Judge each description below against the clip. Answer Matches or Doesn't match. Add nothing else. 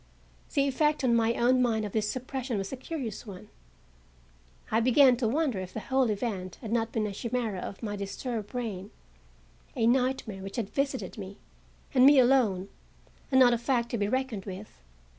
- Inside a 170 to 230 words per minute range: Matches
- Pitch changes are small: Doesn't match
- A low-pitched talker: Doesn't match